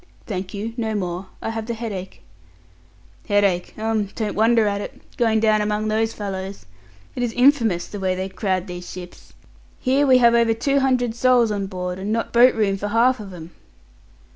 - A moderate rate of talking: Yes, average, 190 wpm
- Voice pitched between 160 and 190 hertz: No, high, 215 Hz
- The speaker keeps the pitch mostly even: No, average, 3.4 semitones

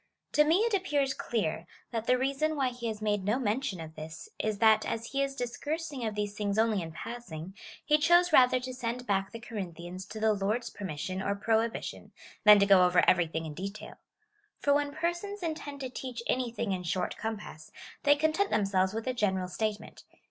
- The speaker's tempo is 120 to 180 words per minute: No, average, 200 wpm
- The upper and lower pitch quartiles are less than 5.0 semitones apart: No, wide, 5.6 semitones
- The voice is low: No, high, 225 Hz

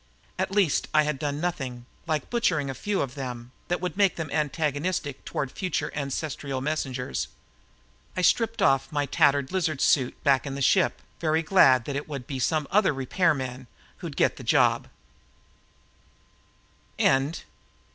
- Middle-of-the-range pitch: Yes, medium, 145 Hz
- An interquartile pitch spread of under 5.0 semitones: Yes, average, 4.0 semitones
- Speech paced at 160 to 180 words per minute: No, average, 150 wpm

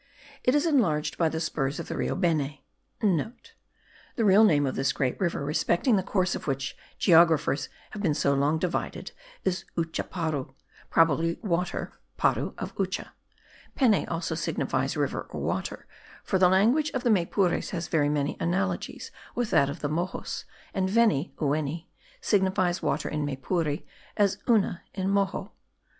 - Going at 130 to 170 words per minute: Yes, average, 155 wpm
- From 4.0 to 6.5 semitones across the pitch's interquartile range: Yes, average, 4.6 semitones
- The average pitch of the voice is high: No, medium, 170 Hz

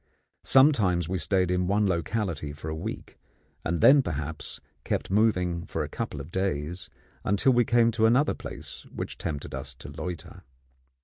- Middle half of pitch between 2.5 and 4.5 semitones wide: No, wide, 5.6 semitones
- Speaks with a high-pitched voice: No, very low, 90 Hz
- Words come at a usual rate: Yes, average, 165 wpm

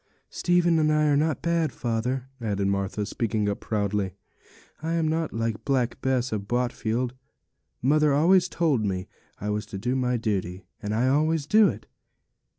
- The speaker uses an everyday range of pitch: No, wide, 6.5 semitones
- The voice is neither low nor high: No, low, 125 Hz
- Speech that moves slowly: No, average, 165 wpm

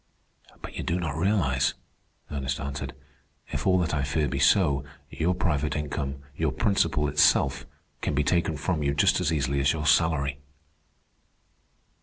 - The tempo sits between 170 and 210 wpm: No, average, 155 wpm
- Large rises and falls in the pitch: No, average, 3.0 semitones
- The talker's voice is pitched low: Yes, very low, 75 Hz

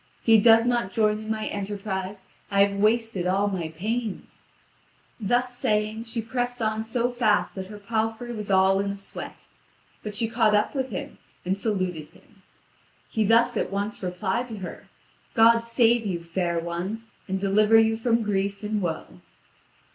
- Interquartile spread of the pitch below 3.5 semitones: Yes, average, 2.8 semitones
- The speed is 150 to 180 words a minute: Yes, average, 170 wpm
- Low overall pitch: No, high, 215 Hz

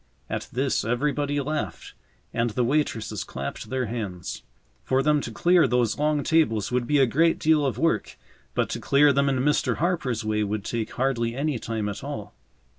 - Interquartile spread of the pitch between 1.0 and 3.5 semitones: No, average, 4.9 semitones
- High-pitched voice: No, low, 130 Hz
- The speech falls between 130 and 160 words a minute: No, average, 185 wpm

